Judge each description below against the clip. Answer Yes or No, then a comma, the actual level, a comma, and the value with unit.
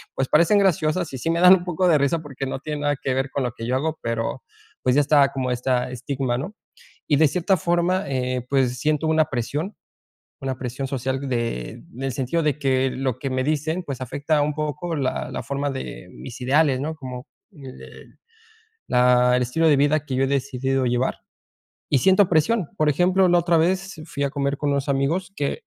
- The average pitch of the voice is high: No, medium, 140 Hz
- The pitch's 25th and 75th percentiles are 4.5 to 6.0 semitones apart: No, average, 3.6 semitones